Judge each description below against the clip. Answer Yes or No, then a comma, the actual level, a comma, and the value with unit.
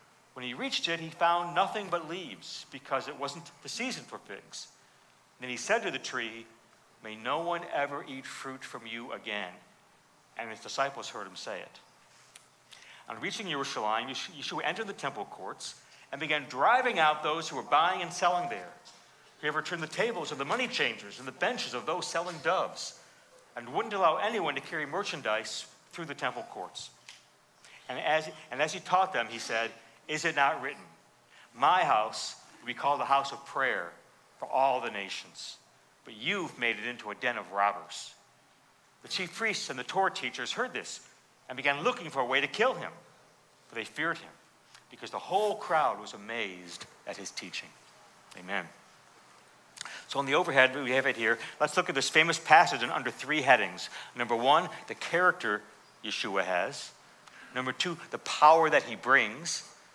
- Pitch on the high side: No, low, 135 Hz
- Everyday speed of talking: Yes, average, 180 wpm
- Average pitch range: No, wide, 6.2 semitones